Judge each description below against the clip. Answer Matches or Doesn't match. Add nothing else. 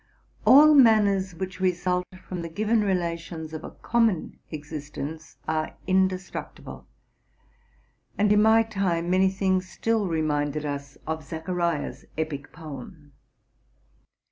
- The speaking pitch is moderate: Matches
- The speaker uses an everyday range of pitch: Matches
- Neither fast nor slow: Doesn't match